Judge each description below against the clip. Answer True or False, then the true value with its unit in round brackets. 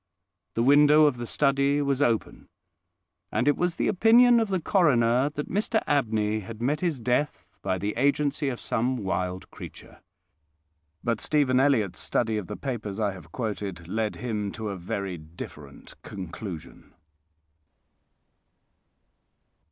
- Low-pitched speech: True (120 Hz)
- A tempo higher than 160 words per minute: False (140 wpm)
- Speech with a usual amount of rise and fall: False (6.0 semitones)